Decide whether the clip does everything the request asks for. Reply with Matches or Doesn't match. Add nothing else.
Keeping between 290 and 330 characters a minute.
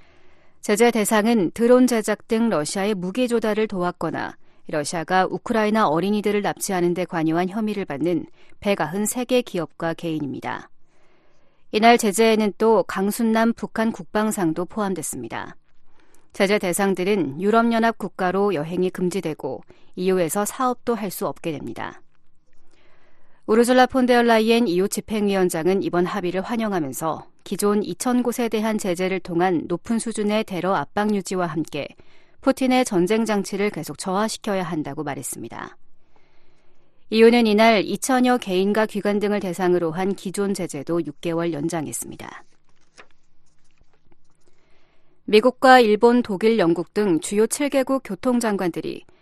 Matches